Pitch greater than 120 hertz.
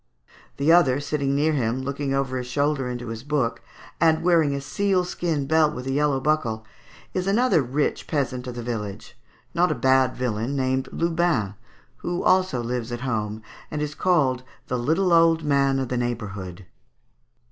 Yes: low, 135 Hz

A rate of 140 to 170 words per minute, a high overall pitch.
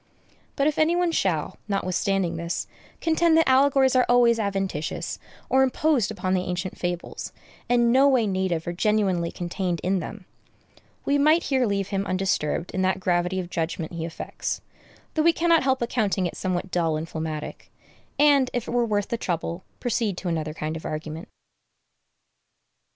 Yes: average, 165 wpm; high, 195 Hz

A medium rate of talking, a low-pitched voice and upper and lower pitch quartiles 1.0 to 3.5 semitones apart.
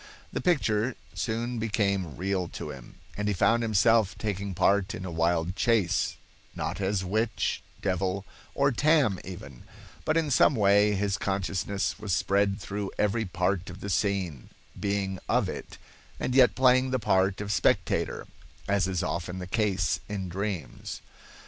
Yes: average, 155 wpm; low, 100 Hz; average, 2.8 semitones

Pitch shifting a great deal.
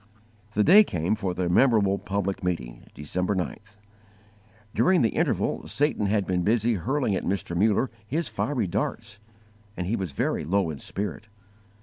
No: average, 3.8 semitones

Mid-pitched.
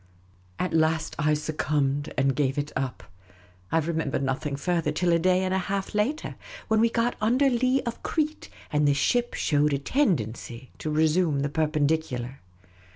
Yes: medium, 155 Hz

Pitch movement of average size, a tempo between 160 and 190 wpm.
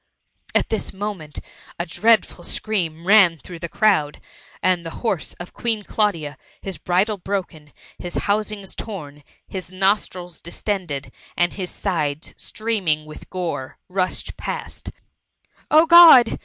No: average, 4.2 semitones; slow, 135 wpm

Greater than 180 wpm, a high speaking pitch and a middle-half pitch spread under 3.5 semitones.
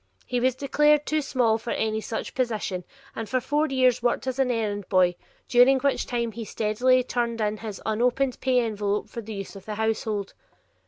Yes: average, 195 wpm; high, 235 Hz; average, 3.1 semitones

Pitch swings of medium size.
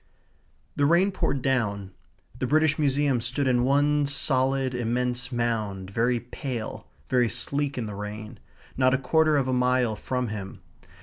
Yes: average, 3.1 semitones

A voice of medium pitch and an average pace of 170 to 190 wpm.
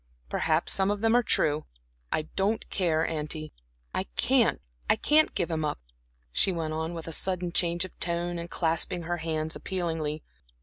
Yes: medium, 170 Hz; average, 175 wpm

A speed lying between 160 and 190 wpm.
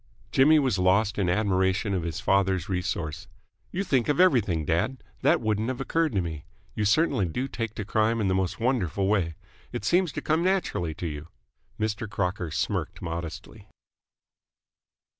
Yes: average, 165 wpm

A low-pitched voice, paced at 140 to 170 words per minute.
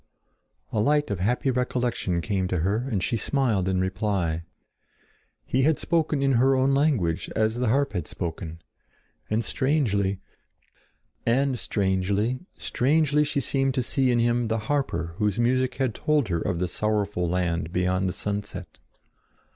Yes: low, 110 Hz; average, 145 wpm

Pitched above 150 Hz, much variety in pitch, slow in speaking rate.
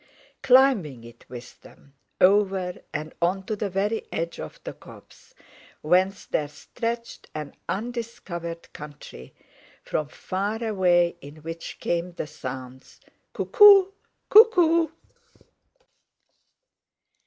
Yes: medium, 185 Hz; wide, 6.9 semitones; slow, 105 wpm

